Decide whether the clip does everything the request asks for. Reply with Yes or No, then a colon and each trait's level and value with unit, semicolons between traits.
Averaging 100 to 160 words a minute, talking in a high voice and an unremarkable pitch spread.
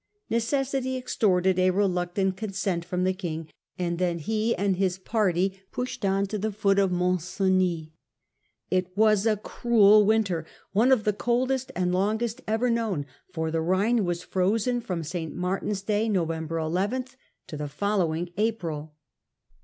Yes: average, 155 wpm; high, 195 Hz; average, 3.6 semitones